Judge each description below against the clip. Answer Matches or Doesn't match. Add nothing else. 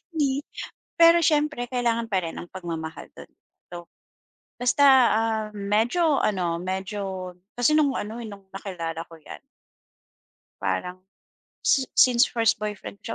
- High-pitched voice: Matches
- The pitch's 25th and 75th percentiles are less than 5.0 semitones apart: Doesn't match